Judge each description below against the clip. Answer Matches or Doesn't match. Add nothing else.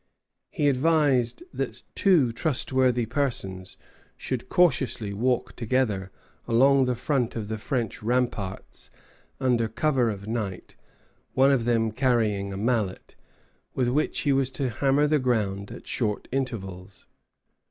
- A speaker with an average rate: Doesn't match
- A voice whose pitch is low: Matches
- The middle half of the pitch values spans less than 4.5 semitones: Matches